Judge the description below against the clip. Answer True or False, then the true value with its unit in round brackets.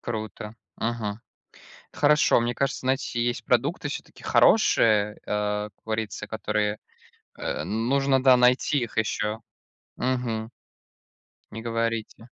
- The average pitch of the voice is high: False (115 Hz)